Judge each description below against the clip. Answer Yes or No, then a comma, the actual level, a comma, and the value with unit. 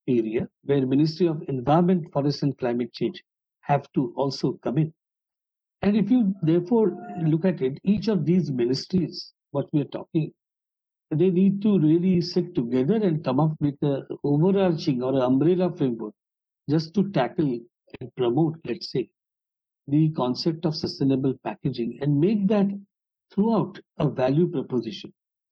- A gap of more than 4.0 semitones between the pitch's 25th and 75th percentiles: Yes, average, 5.1 semitones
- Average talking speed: Yes, average, 150 wpm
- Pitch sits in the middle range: Yes, medium, 155 Hz